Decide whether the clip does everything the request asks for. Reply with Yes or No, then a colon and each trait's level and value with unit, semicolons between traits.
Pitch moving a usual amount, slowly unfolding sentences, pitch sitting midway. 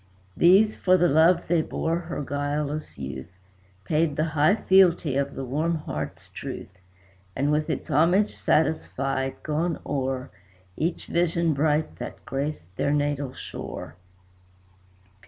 Yes: average, 3.5 semitones; slow, 130 wpm; medium, 150 Hz